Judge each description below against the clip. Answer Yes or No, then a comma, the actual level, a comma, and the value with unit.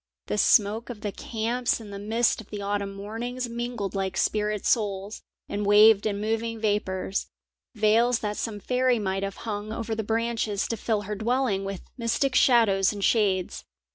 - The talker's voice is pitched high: Yes, high, 215 Hz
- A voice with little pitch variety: Yes, narrow, 2.3 semitones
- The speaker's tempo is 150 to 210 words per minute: Yes, average, 170 wpm